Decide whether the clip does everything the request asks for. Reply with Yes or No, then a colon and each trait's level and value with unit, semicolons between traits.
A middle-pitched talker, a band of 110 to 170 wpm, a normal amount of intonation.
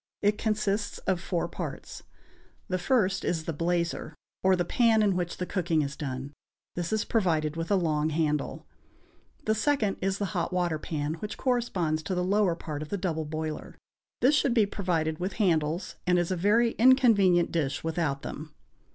No: medium, 180 Hz; average, 180 wpm; average, 4.4 semitones